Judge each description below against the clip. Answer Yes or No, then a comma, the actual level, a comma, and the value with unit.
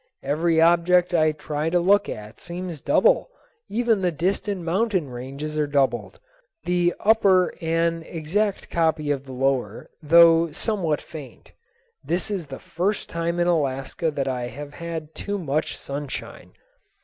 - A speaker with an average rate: Yes, average, 145 wpm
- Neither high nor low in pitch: Yes, medium, 165 Hz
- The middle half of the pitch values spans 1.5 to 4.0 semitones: Yes, average, 3.6 semitones